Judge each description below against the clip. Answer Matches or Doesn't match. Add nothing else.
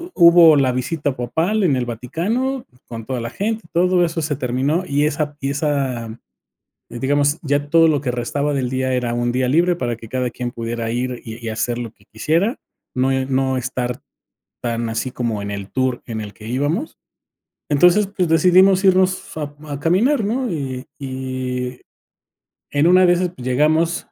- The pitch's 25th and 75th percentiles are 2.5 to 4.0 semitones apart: Doesn't match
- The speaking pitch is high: Doesn't match